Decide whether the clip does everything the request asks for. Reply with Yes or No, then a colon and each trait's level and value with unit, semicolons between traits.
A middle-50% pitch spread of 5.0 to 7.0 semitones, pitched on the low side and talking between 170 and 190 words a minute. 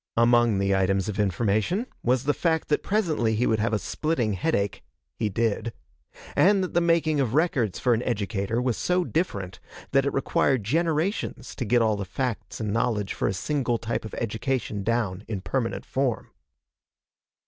Yes: wide, 5.4 semitones; low, 115 Hz; average, 175 wpm